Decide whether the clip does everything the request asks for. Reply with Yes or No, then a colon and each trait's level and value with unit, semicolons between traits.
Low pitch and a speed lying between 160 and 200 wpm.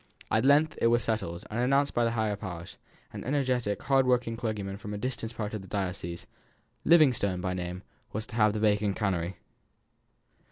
Yes: low, 110 Hz; average, 185 wpm